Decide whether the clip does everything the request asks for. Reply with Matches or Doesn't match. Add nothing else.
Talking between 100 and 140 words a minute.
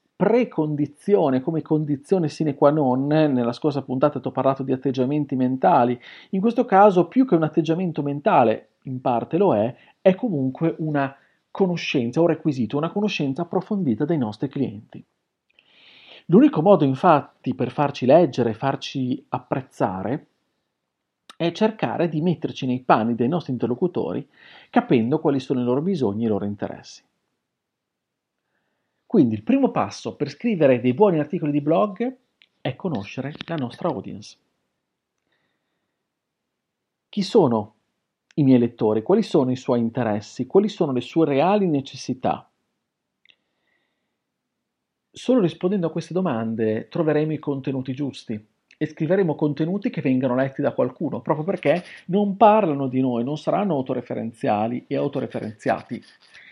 Matches